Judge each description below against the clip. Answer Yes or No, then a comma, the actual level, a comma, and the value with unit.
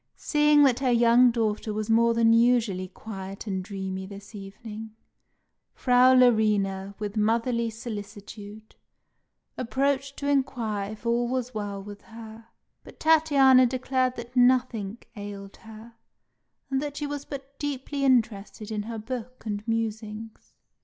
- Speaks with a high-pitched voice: Yes, high, 230 Hz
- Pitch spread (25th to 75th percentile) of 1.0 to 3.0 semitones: No, average, 3.4 semitones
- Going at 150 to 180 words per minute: No, slow, 135 wpm